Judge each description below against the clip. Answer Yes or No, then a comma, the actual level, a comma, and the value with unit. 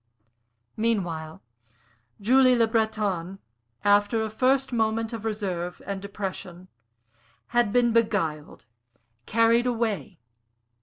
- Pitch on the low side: No, high, 220 Hz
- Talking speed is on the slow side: Yes, slow, 95 wpm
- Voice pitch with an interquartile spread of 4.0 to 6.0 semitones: No, average, 3.1 semitones